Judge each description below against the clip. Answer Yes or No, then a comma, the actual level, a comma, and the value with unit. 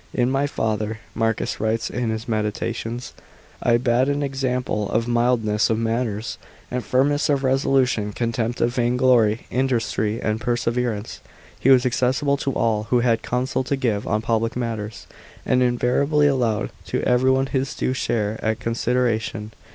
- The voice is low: Yes, low, 120 Hz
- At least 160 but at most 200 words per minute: Yes, average, 165 wpm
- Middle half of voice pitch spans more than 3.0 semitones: No, narrow, 2.5 semitones